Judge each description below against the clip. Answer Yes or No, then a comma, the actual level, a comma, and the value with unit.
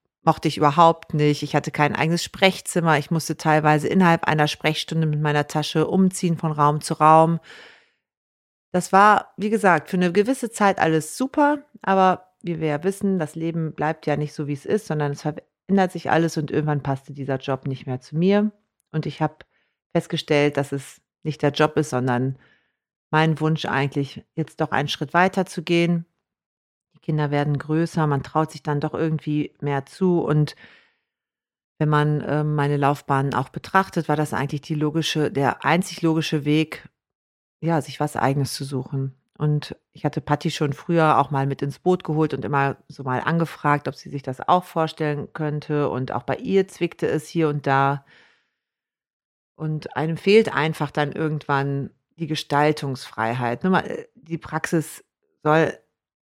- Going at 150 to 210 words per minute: Yes, average, 170 wpm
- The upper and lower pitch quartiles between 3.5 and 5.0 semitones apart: No, narrow, 2.6 semitones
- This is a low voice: No, medium, 155 Hz